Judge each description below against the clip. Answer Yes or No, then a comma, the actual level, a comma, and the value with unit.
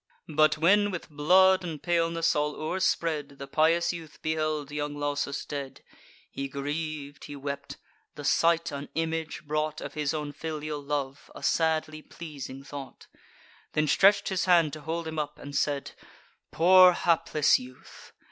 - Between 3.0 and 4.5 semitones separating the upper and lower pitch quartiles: No, narrow, 2.4 semitones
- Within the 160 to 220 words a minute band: No, average, 150 wpm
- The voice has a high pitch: No, medium, 155 Hz